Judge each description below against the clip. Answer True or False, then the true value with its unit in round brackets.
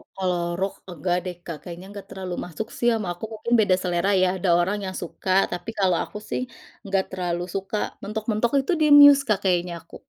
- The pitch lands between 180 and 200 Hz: True (190 Hz)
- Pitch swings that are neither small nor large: True (3.1 semitones)